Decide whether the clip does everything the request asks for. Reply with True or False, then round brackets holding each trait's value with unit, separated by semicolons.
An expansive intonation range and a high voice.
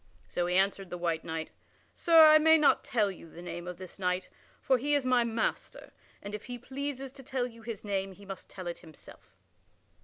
True (6.4 semitones; 205 Hz)